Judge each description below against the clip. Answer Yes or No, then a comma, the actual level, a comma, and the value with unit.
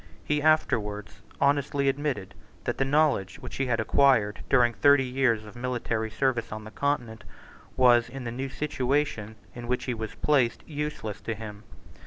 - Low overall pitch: Yes, low, 125 Hz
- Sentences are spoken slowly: No, average, 165 wpm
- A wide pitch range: No, average, 4.0 semitones